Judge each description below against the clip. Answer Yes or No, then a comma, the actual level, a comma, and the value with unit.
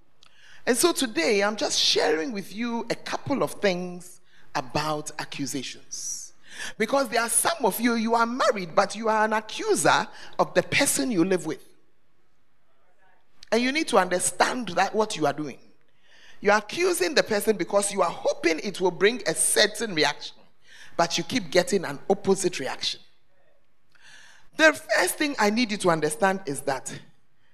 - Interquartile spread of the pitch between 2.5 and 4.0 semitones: No, wide, 5.5 semitones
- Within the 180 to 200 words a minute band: No, average, 165 wpm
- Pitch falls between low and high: No, high, 200 Hz